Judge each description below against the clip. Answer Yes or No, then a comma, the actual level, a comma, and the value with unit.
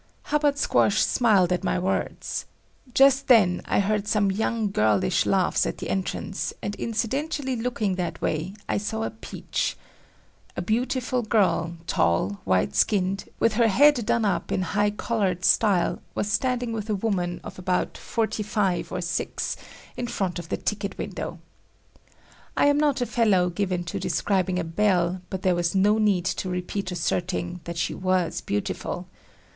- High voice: Yes, high, 200 Hz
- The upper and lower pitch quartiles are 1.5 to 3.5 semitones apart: No, average, 4.0 semitones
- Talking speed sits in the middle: Yes, average, 160 wpm